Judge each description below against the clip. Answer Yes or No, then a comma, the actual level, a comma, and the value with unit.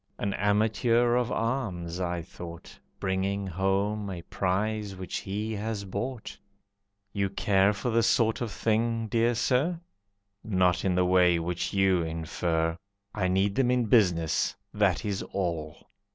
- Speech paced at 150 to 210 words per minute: No, average, 140 wpm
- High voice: No, low, 100 Hz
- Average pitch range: Yes, average, 3.6 semitones